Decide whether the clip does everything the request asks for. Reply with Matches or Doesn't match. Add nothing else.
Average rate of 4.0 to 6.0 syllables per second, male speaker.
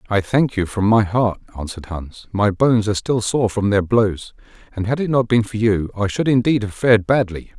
Matches